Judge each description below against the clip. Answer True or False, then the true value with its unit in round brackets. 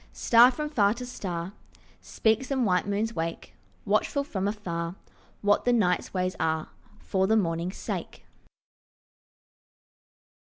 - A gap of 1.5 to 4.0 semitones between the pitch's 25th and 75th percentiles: False (4.5 semitones)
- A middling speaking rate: False (125 wpm)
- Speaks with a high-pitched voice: True (205 Hz)